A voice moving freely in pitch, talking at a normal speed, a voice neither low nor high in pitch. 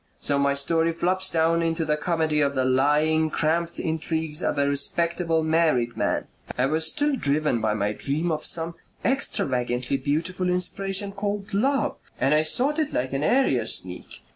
No: average, 3.8 semitones; average, 165 wpm; medium, 160 Hz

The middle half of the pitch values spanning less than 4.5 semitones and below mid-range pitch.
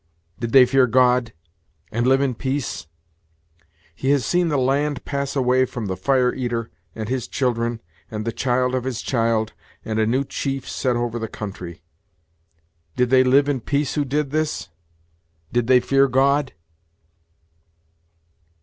Yes: average, 2.7 semitones; low, 125 Hz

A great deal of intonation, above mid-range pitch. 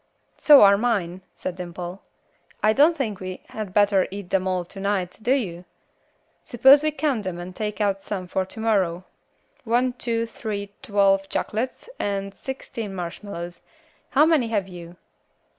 No: average, 3.8 semitones; high, 200 Hz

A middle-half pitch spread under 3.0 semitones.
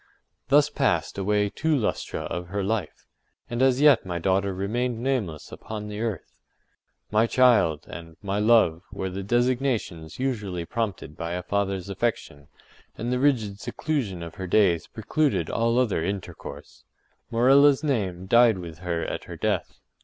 No: average, 5.2 semitones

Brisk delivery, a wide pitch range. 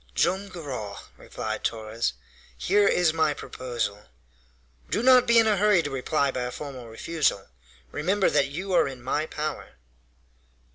No: average, 150 wpm; wide, 7.3 semitones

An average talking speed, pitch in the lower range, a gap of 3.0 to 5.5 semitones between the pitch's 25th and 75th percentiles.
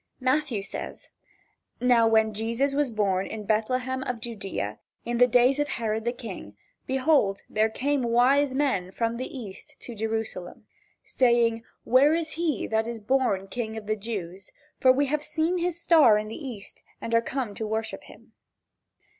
No: average, 170 wpm; high, 235 Hz; average, 3.6 semitones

